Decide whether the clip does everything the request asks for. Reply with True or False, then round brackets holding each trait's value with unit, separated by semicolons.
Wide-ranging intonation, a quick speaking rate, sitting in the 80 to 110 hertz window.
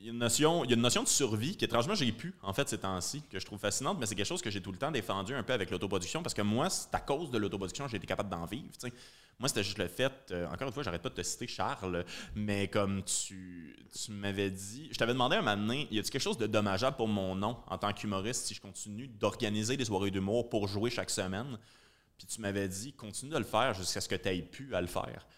False (3.8 semitones; 285 wpm; 105 Hz)